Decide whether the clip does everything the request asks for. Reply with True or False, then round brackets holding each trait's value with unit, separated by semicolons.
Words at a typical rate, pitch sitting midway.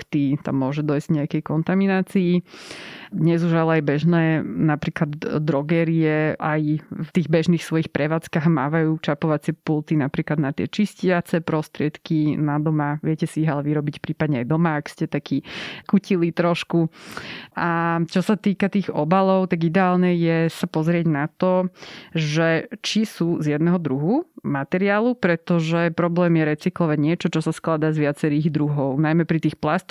True (155 wpm; 165 Hz)